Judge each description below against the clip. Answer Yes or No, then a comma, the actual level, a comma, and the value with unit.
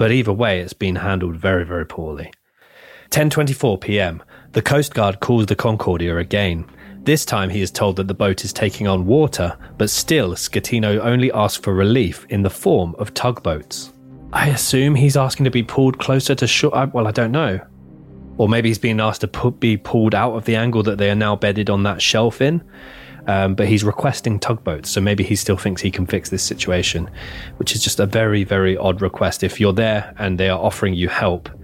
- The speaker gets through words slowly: No, fast, 205 wpm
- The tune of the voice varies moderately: Yes, average, 4.0 semitones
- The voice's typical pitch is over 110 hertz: No, low, 105 Hz